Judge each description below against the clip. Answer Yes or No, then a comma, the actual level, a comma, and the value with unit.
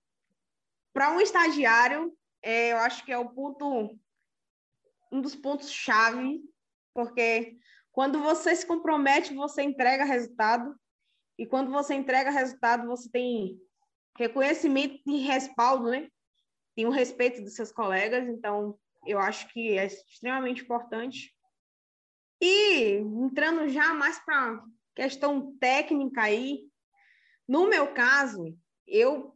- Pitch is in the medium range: No, very high, 260 Hz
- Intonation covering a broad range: No, average, 3.7 semitones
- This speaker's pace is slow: Yes, slow, 115 wpm